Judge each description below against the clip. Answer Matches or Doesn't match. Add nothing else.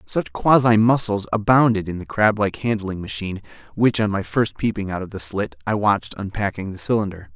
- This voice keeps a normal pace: Matches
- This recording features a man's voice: Matches